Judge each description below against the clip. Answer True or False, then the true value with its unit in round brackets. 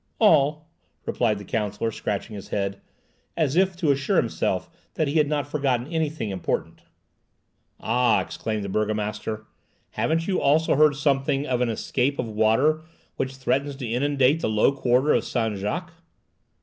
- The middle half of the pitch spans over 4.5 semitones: True (5.5 semitones)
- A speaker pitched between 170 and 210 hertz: False (135 Hz)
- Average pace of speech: True (155 wpm)